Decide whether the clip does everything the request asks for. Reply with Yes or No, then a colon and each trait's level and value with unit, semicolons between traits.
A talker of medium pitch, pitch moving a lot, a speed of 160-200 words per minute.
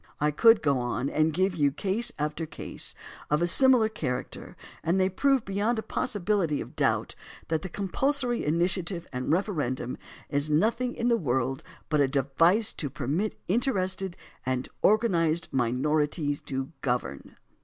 No: medium, 165 Hz; wide, 6.4 semitones; average, 150 wpm